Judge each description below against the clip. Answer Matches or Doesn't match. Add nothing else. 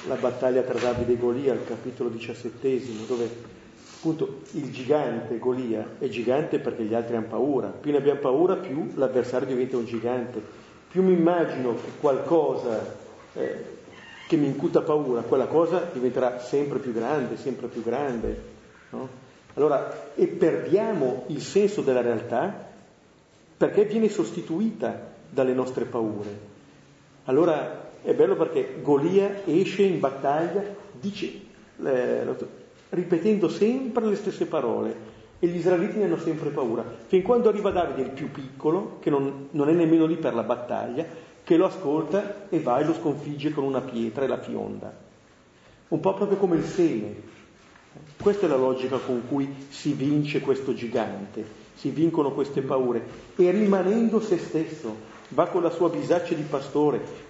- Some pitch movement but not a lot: Doesn't match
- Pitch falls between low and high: Matches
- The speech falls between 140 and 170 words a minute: Matches